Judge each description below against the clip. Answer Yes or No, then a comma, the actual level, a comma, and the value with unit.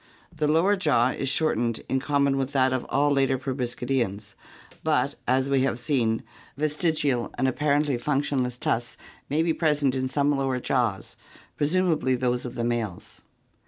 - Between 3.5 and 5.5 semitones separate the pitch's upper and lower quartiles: No, average, 3.0 semitones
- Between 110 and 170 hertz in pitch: Yes, low, 135 Hz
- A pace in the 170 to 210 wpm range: No, average, 155 wpm